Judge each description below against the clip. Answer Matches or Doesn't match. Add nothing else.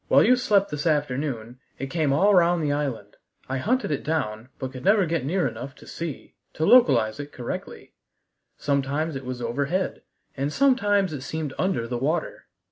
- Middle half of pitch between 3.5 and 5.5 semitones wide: Matches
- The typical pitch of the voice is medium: Matches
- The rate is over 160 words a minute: Matches